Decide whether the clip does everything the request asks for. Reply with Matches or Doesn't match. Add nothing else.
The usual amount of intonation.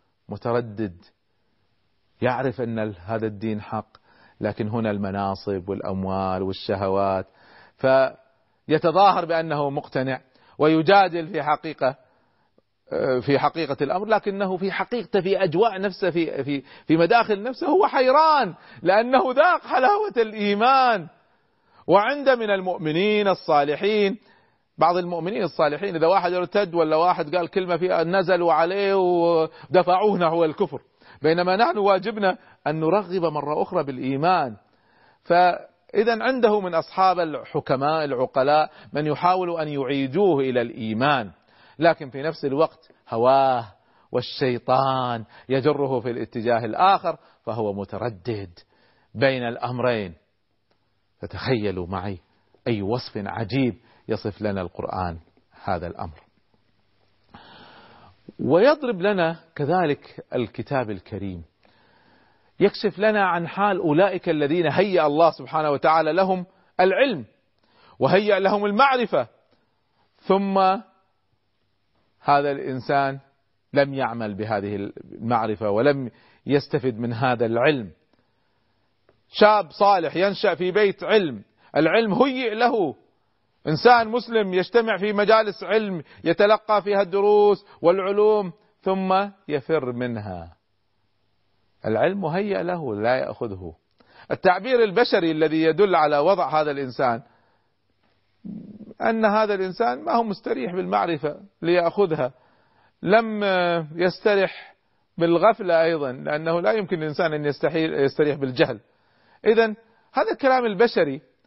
Doesn't match